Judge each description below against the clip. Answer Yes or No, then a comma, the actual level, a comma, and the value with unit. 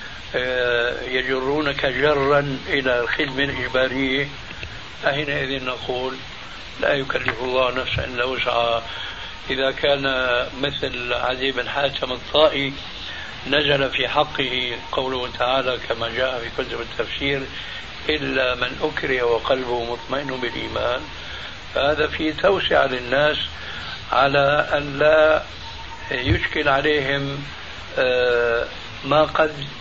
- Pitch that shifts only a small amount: Yes, narrow, 2.3 semitones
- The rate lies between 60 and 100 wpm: Yes, average, 95 wpm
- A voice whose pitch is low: Yes, low, 130 Hz